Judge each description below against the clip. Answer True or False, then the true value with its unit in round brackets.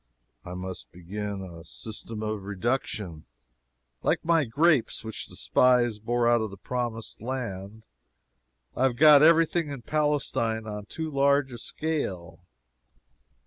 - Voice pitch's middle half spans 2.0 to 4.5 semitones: False (5.5 semitones)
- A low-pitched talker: True (115 Hz)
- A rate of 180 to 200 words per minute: False (140 wpm)